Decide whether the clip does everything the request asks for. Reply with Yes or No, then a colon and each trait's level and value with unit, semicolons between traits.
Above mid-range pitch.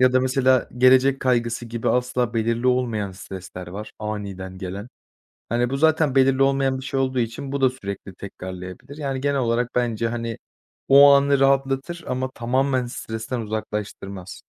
No: low, 125 Hz